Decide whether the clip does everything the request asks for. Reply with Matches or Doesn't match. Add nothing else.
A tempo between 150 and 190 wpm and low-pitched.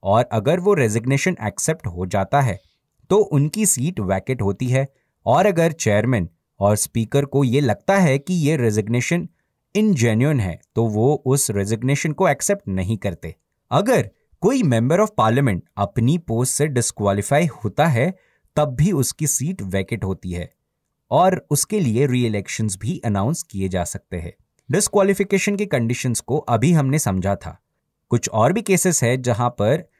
Matches